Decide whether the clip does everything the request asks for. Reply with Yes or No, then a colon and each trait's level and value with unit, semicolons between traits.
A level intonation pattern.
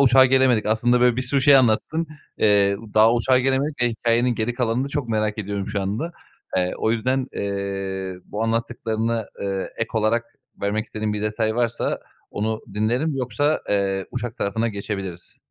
No: average, 3.2 semitones